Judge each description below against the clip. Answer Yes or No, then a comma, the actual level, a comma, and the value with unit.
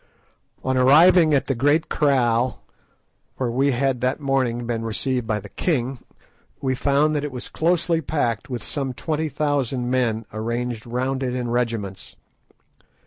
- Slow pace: No, average, 150 wpm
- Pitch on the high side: No, low, 130 Hz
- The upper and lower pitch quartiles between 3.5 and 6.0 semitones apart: No, average, 3.1 semitones